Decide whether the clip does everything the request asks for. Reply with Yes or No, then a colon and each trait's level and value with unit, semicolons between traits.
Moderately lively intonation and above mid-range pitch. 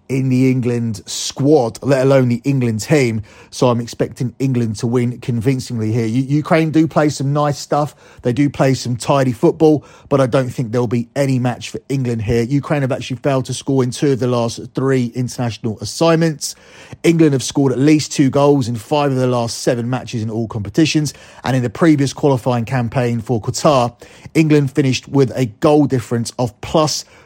No: average, 3.2 semitones; low, 130 Hz